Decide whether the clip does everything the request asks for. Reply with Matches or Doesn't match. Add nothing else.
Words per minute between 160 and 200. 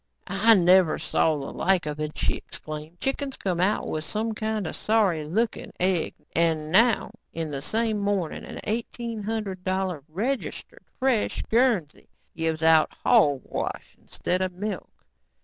Doesn't match